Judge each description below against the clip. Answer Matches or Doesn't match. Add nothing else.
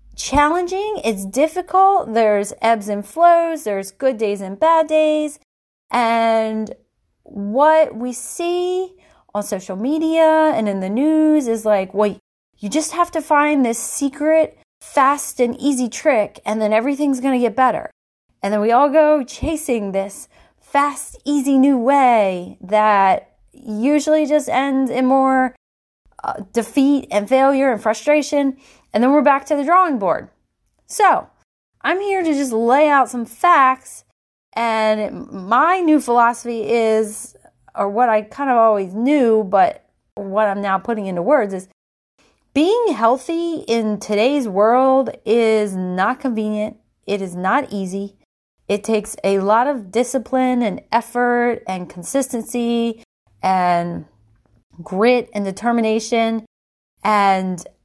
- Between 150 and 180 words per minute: Doesn't match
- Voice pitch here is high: Matches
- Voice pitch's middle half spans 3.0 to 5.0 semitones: Doesn't match